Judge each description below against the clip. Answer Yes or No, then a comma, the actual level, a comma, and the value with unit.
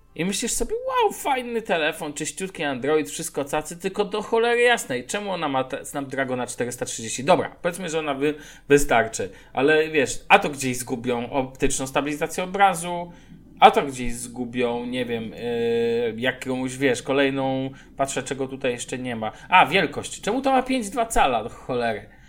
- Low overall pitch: No, medium, 150 Hz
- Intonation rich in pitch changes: Yes, wide, 7.0 semitones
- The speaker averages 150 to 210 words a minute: Yes, average, 155 wpm